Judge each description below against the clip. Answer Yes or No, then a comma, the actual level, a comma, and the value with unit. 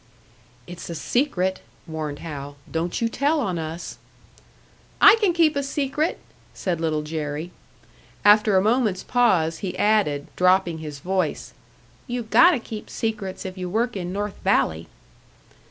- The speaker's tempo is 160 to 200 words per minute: No, average, 140 wpm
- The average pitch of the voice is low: No, high, 190 Hz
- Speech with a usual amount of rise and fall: No, wide, 6.1 semitones